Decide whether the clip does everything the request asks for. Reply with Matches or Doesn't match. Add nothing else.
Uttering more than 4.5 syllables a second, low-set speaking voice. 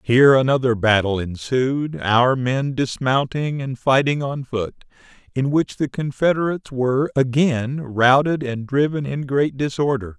Doesn't match